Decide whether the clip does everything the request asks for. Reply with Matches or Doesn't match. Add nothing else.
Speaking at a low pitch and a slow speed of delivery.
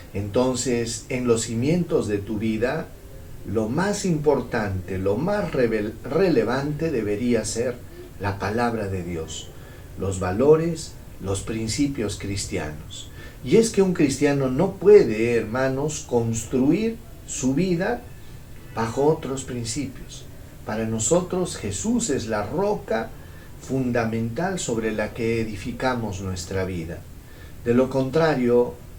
Matches